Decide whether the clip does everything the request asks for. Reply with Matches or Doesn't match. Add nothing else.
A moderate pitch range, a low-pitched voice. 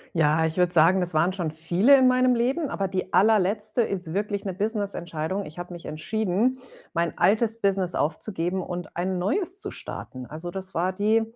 Doesn't match